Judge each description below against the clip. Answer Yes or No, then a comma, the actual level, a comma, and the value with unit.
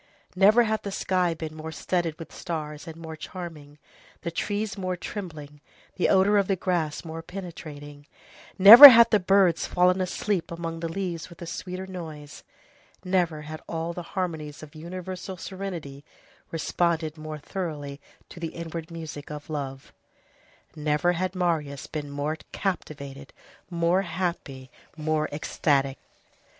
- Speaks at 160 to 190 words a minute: No, average, 140 wpm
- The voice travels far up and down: No, average, 3.3 semitones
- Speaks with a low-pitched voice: No, medium, 165 Hz